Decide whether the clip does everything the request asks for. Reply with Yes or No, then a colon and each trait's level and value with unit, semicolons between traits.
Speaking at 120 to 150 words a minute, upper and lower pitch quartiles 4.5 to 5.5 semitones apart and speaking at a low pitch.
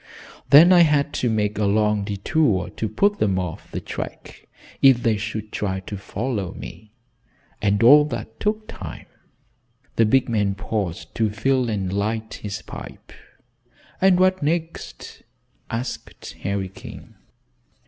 Yes: average, 140 wpm; average, 5.1 semitones; low, 110 Hz